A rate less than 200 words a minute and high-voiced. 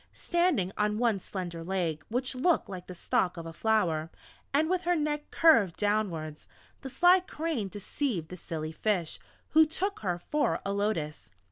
Yes: average, 165 wpm; high, 205 Hz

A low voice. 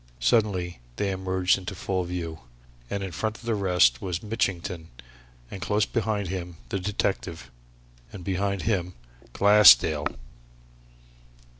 Yes: very low, 95 Hz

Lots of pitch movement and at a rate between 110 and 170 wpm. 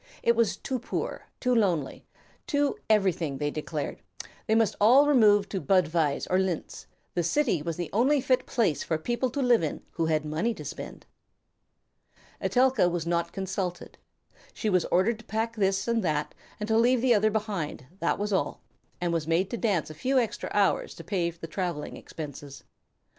No: wide, 5.7 semitones; average, 180 wpm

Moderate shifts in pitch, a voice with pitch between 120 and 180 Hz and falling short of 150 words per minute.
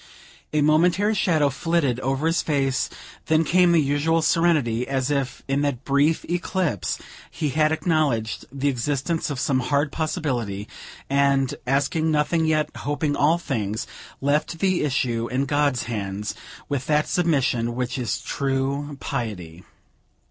Yes: average, 3.6 semitones; medium, 140 Hz; average, 140 wpm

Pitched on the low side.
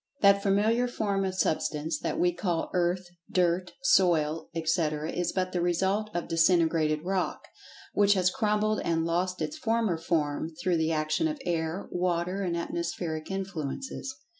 No: medium, 175 Hz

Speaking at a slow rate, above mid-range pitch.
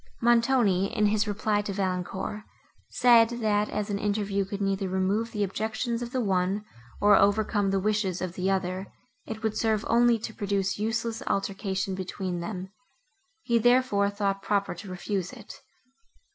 No: average, 160 wpm; high, 205 Hz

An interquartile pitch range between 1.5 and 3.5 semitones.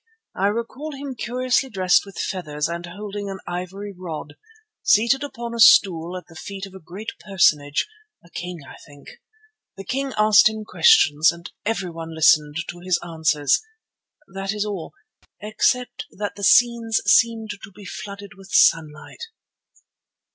No: average, 4.8 semitones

